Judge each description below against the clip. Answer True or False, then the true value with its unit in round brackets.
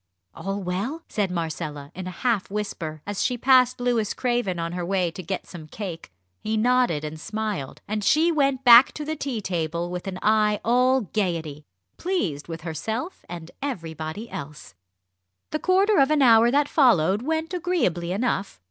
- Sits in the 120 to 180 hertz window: False (210 Hz)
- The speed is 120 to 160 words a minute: False (170 wpm)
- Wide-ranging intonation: True (6.8 semitones)